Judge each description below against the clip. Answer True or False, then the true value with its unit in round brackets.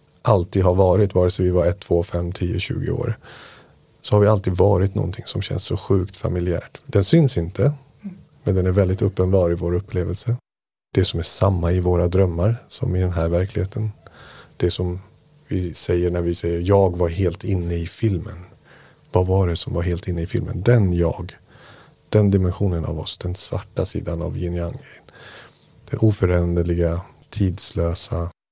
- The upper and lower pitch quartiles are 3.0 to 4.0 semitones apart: True (3.7 semitones)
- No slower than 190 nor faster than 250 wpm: False (180 wpm)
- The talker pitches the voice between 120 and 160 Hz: False (95 Hz)